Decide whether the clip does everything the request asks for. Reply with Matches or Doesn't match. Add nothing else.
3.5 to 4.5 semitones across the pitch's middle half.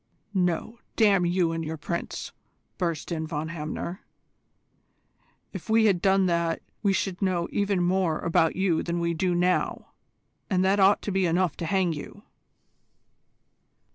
Doesn't match